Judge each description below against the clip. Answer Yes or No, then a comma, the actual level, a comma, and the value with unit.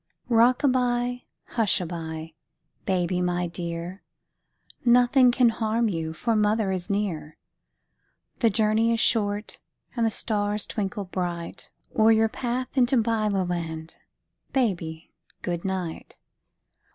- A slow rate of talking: Yes, slow, 120 wpm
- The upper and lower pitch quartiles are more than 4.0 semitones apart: Yes, average, 4.8 semitones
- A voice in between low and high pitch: No, high, 210 Hz